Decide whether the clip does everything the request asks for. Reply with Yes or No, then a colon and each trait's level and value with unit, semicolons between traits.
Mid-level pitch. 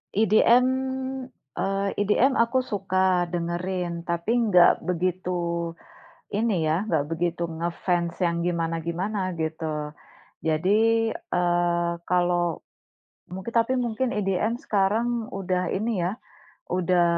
Yes: medium, 180 Hz